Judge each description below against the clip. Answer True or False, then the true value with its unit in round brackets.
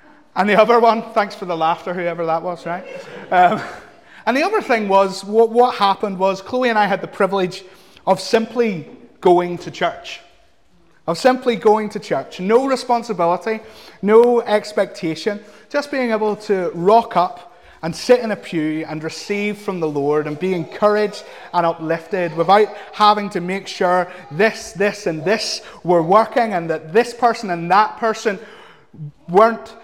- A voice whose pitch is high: True (205 Hz)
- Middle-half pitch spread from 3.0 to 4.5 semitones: True (4.0 semitones)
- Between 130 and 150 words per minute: False (165 wpm)